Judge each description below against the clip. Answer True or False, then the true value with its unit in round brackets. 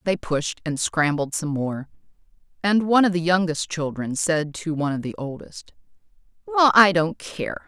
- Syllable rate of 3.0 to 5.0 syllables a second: True (4.7 syllables/s)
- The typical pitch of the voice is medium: True (160 Hz)